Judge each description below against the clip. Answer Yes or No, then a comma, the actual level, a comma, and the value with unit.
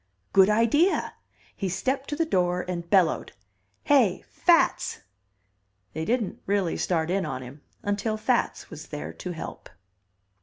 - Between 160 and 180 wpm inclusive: No, average, 140 wpm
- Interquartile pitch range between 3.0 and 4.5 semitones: No, average, 5.1 semitones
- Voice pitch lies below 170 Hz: No, high, 190 Hz